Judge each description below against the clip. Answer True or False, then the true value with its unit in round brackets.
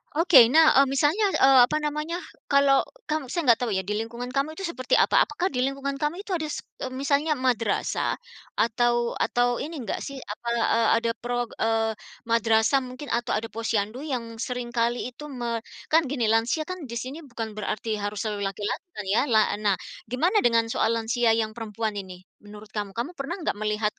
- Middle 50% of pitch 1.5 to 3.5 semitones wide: False (3.9 semitones)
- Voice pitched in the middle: False (240 Hz)